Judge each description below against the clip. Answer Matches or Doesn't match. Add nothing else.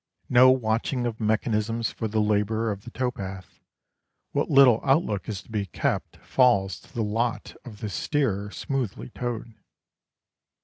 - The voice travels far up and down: Doesn't match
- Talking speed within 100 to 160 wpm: Matches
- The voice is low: Matches